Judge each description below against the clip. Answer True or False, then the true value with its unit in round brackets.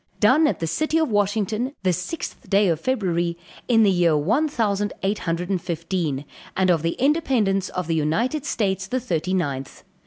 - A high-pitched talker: True (195 Hz)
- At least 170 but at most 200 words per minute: True (185 wpm)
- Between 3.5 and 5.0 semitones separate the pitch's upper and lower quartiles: False (5.4 semitones)